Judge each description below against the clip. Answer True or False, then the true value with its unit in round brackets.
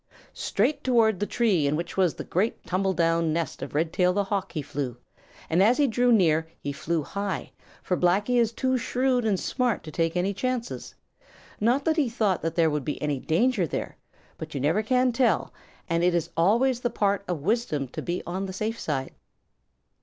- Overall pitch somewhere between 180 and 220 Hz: True (190 Hz)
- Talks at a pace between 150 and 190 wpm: False (200 wpm)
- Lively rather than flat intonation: True (6.1 semitones)